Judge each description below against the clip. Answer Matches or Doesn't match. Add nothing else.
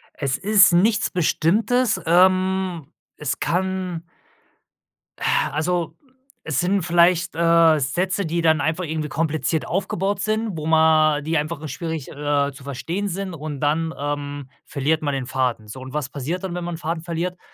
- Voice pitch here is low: Doesn't match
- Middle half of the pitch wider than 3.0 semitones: Matches